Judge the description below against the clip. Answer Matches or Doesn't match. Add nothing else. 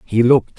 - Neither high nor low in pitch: Doesn't match